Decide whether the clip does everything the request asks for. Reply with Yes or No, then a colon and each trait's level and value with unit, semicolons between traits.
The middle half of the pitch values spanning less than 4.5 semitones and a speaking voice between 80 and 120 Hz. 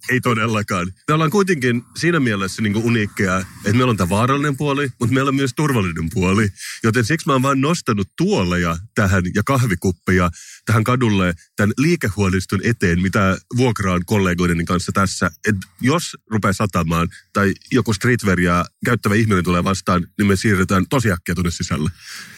No: average, 5.0 semitones; low, 105 Hz